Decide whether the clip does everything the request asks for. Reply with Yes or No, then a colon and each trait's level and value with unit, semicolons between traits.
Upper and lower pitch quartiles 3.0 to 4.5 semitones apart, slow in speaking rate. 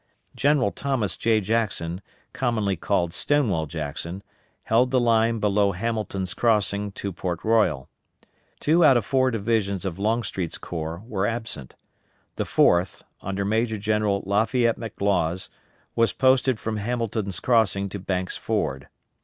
Yes: average, 3.5 semitones; slow, 130 wpm